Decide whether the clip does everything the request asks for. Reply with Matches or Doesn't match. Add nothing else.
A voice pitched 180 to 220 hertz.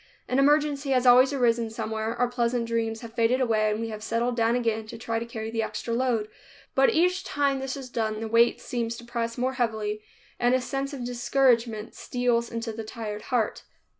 Doesn't match